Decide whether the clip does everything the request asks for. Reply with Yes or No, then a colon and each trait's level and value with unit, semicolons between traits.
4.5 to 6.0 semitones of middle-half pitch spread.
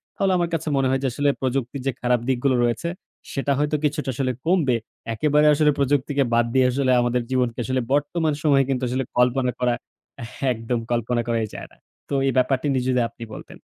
No: average, 2.7 semitones